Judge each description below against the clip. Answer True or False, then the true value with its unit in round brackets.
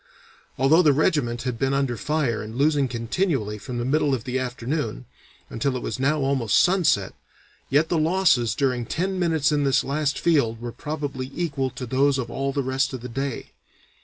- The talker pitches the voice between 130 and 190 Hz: True (135 Hz)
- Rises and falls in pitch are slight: False (3.6 semitones)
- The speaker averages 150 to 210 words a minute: True (190 wpm)